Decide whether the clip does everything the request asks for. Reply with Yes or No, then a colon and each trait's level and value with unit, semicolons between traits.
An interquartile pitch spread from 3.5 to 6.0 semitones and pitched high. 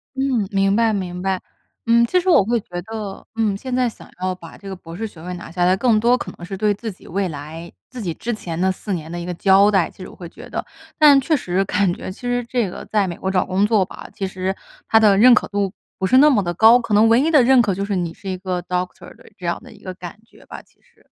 Yes: average, 3.9 semitones; high, 195 Hz